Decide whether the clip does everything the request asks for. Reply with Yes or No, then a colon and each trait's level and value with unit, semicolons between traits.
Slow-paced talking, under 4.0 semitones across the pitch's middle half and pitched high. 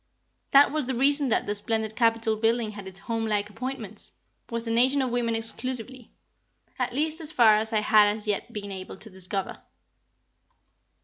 No: average, 180 wpm; average, 3.2 semitones; high, 225 Hz